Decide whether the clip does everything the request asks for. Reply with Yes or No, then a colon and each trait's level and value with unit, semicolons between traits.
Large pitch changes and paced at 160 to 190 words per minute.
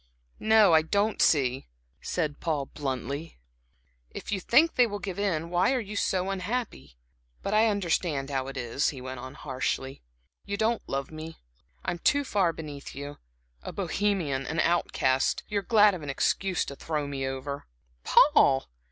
Yes: wide, 6.7 semitones; average, 170 wpm